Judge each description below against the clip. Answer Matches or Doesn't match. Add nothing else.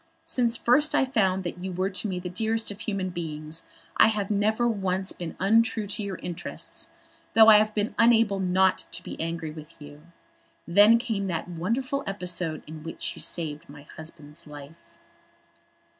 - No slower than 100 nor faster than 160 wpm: Doesn't match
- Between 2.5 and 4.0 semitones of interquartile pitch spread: Doesn't match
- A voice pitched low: Doesn't match